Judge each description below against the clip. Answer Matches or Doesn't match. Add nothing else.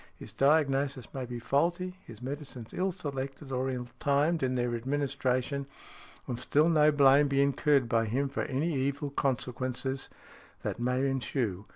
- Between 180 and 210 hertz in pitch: Doesn't match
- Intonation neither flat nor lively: Doesn't match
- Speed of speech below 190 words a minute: Matches